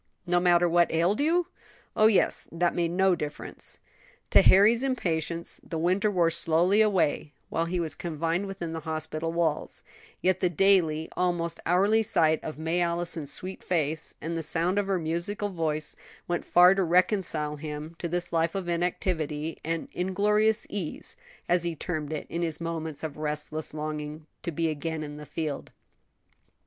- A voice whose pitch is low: No, medium, 170 Hz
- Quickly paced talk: No, average, 165 wpm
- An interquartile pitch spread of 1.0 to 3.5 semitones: Yes, narrow, 2.5 semitones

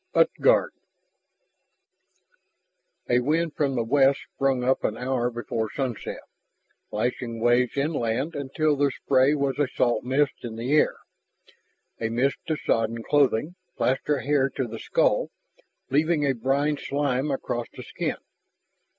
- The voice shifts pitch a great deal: No, average, 3.1 semitones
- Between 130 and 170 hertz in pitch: Yes, low, 135 Hz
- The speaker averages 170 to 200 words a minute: No, slow, 135 wpm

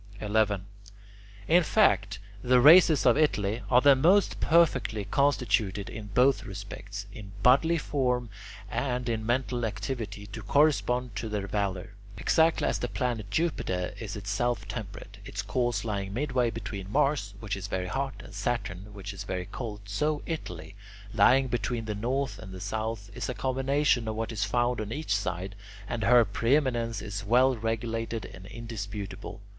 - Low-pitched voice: Yes, low, 110 Hz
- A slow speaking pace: No, average, 160 wpm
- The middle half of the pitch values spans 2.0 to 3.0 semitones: No, average, 3.8 semitones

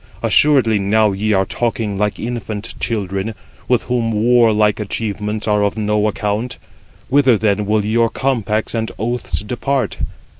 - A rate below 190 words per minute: Yes, average, 140 wpm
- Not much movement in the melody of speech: Yes, narrow, 2.1 semitones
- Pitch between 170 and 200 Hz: No, low, 110 Hz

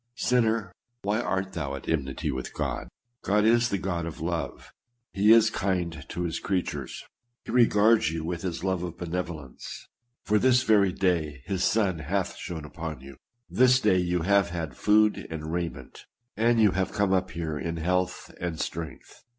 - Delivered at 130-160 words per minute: No, average, 175 wpm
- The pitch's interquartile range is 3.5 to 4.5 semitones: Yes, average, 4.2 semitones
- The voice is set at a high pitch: No, very low, 90 Hz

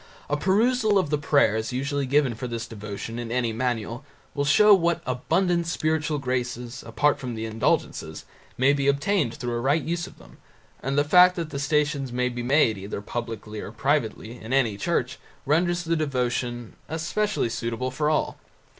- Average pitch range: Yes, average, 4.7 semitones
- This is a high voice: No, low, 135 Hz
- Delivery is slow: No, average, 175 wpm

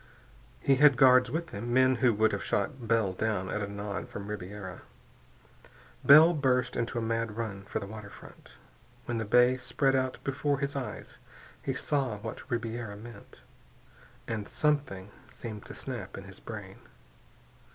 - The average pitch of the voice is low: Yes, low, 115 Hz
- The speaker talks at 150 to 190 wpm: Yes, average, 160 wpm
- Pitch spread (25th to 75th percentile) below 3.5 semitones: No, average, 3.9 semitones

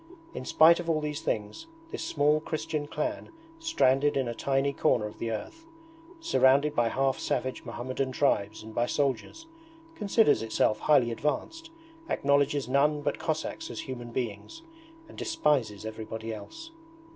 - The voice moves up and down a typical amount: Yes, average, 4.9 semitones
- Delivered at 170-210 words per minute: No, average, 145 wpm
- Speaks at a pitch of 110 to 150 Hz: Yes, medium, 140 Hz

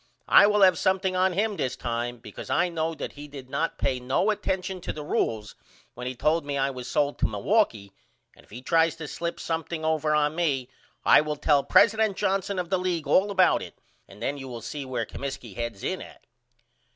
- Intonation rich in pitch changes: Yes, wide, 6.0 semitones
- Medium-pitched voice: Yes, medium, 150 Hz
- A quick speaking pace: Yes, fast, 215 wpm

